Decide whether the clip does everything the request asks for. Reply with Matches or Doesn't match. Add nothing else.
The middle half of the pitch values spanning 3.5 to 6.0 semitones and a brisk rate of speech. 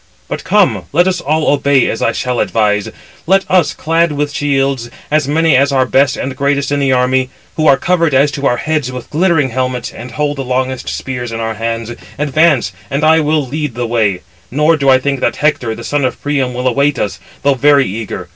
Doesn't match